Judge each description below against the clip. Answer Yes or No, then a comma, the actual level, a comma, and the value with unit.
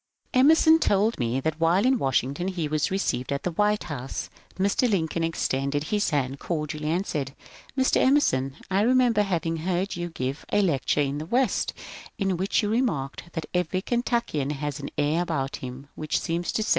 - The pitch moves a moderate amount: No, wide, 6.1 semitones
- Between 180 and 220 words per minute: Yes, average, 185 wpm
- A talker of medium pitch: Yes, medium, 165 Hz